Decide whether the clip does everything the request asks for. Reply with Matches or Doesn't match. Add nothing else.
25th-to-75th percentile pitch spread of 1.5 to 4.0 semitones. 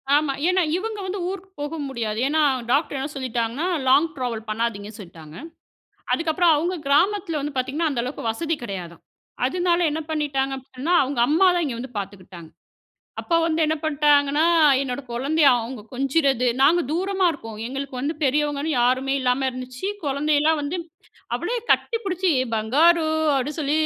Doesn't match